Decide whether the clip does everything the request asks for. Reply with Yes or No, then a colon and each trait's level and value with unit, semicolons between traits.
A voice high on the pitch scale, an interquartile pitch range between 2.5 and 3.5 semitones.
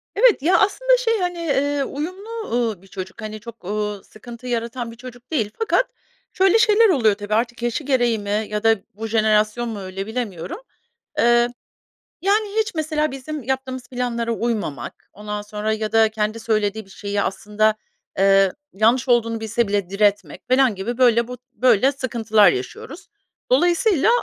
No: high, 235 Hz; average, 4.3 semitones